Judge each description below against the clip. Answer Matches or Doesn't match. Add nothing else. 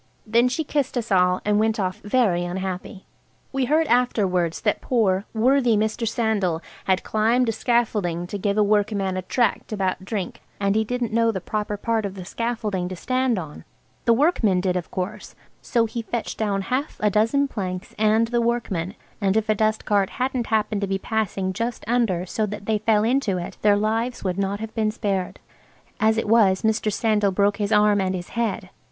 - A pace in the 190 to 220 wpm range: Matches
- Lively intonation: Doesn't match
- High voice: Matches